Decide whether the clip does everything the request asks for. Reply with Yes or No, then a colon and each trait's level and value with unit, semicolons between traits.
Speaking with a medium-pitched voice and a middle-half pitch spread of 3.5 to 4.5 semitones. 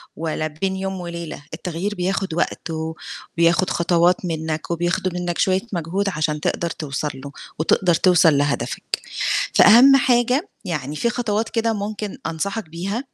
Yes: medium, 175 Hz; average, 3.8 semitones